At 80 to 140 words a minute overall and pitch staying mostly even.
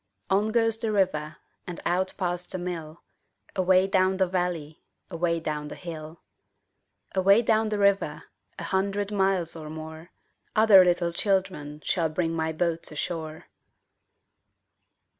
No: slow, 135 wpm; average, 3.3 semitones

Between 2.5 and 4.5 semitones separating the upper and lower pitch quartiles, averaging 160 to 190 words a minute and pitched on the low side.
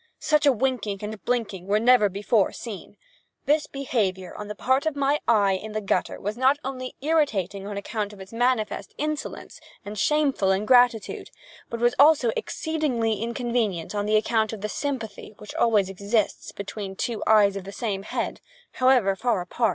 No: average, 4.1 semitones; average, 170 wpm; high, 220 Hz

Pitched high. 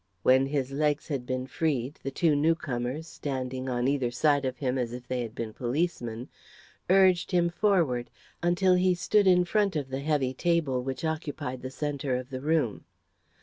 No: medium, 140 Hz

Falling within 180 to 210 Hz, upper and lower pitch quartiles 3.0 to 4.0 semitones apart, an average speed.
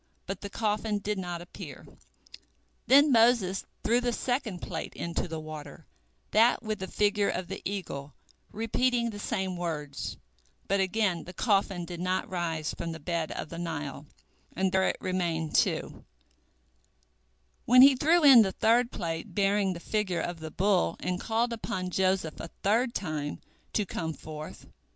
No: high, 190 Hz; average, 4.4 semitones; average, 160 wpm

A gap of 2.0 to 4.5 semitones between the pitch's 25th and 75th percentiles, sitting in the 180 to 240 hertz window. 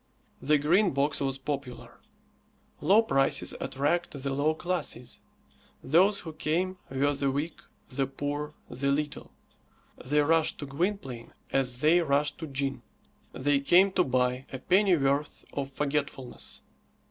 No: average, 3.1 semitones; medium, 145 Hz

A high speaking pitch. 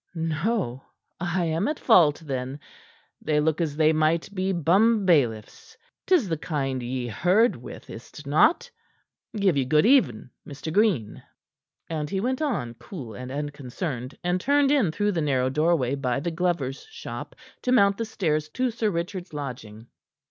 No: medium, 160 Hz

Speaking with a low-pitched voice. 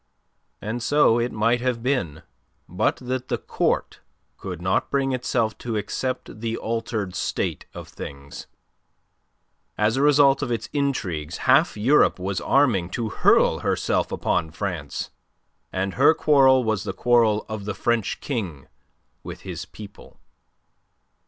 Yes: low, 115 Hz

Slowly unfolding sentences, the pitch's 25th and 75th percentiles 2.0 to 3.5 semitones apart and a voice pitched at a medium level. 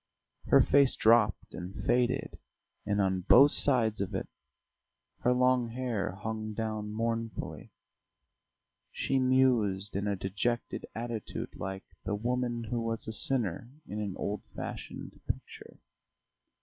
No: slow, 125 wpm; average, 3.1 semitones; low, 110 Hz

